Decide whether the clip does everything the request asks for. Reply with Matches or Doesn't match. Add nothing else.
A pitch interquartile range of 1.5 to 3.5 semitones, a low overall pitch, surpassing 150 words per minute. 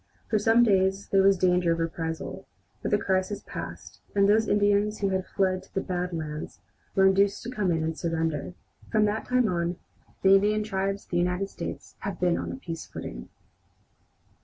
Doesn't match